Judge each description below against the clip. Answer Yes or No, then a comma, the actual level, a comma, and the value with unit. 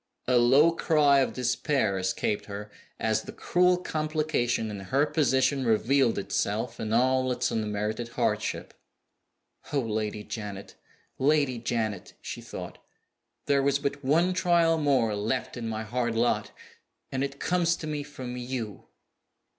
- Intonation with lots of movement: No, average, 4.6 semitones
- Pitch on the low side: Yes, low, 125 Hz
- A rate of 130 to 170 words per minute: Yes, average, 140 wpm